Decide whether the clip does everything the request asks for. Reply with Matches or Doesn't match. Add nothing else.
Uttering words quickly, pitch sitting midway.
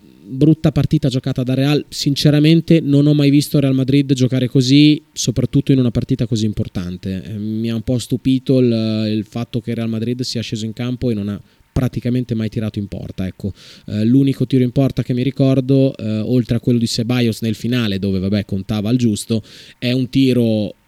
Doesn't match